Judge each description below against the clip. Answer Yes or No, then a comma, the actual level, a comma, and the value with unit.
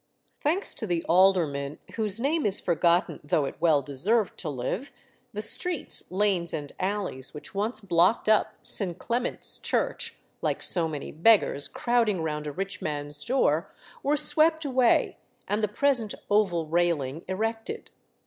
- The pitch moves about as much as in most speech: No, wide, 5.9 semitones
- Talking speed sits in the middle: Yes, average, 150 wpm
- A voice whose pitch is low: No, high, 190 Hz